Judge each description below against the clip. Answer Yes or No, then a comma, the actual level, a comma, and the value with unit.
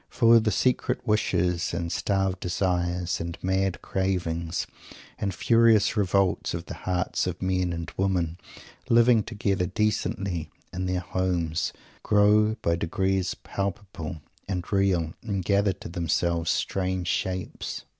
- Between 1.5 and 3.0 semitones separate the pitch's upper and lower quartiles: Yes, narrow, 2.4 semitones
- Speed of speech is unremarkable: No, slow, 125 wpm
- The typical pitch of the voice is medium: No, very low, 95 Hz